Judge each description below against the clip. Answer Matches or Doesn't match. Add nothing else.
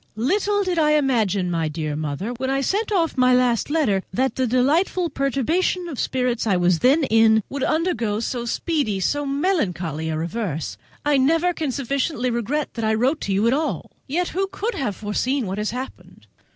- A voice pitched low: Doesn't match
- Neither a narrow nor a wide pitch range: Doesn't match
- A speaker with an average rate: Matches